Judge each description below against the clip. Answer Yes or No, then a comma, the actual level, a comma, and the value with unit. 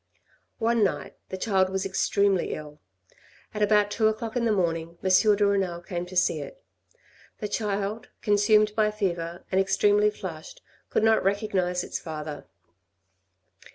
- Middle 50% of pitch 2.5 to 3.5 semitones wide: Yes, average, 2.9 semitones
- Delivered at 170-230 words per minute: No, average, 155 wpm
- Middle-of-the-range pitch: No, high, 200 Hz